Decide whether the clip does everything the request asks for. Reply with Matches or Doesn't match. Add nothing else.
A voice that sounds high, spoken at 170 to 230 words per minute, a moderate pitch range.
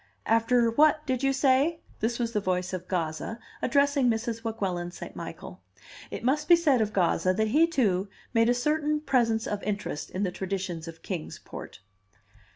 Doesn't match